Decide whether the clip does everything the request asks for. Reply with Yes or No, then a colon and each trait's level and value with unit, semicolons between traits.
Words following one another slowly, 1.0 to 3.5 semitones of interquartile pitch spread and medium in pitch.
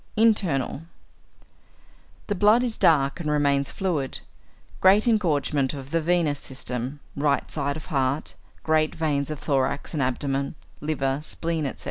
Yes: slow, 130 wpm; average, 3.2 semitones; medium, 150 Hz